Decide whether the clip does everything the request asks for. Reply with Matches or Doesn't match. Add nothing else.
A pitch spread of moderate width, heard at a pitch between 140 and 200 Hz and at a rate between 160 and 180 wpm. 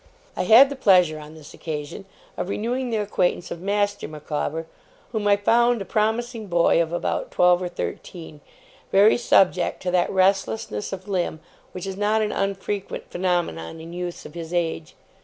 Matches